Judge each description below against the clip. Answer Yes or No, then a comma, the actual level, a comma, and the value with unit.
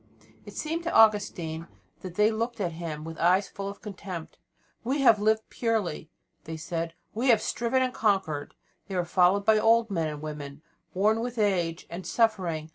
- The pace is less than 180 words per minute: No, average, 185 wpm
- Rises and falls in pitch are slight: No, average, 5.1 semitones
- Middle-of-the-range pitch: No, high, 195 Hz